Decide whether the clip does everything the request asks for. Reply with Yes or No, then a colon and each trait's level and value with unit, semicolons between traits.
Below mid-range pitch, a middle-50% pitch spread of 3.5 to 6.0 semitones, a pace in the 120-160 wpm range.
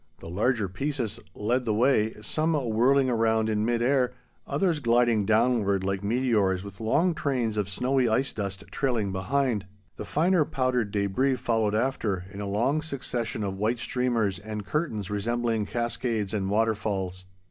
Yes: low, 115 Hz; average, 3.9 semitones; average, 155 wpm